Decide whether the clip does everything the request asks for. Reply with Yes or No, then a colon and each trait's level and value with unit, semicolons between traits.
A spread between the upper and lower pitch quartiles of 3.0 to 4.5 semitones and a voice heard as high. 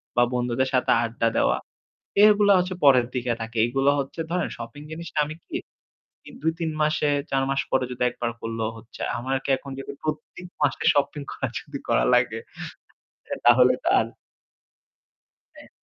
No: average, 4.0 semitones; low, 135 Hz